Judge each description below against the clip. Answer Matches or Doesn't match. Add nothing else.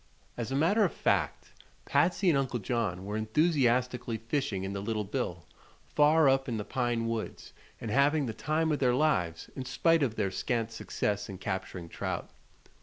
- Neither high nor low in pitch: Doesn't match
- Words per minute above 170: Matches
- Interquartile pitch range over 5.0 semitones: Matches